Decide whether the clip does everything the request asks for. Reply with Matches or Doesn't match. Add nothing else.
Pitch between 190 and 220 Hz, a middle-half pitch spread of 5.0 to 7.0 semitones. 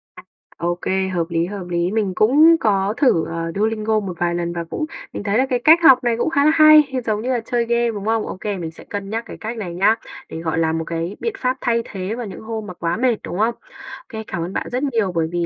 Matches